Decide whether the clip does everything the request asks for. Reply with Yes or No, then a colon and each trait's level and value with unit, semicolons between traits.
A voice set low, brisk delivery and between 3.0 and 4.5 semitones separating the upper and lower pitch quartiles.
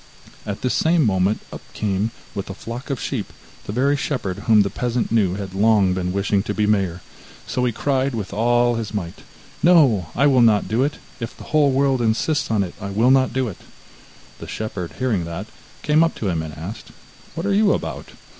No: low, 110 Hz; fast, 210 wpm; average, 5.0 semitones